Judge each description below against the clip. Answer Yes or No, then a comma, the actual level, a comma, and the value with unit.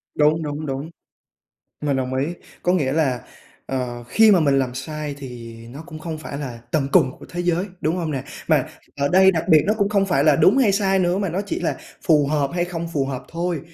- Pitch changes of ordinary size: Yes, average, 4.5 semitones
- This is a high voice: No, medium, 155 Hz